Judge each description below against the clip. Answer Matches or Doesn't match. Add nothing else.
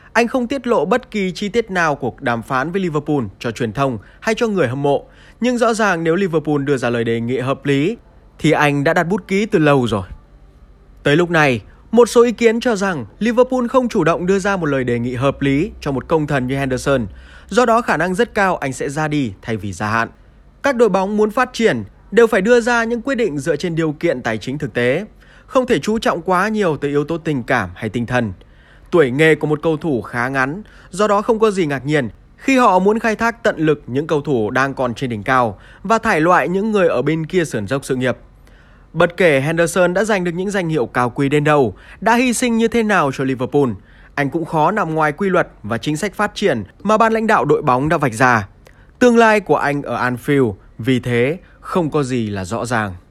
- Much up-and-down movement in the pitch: Matches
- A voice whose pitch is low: Doesn't match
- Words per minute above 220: Matches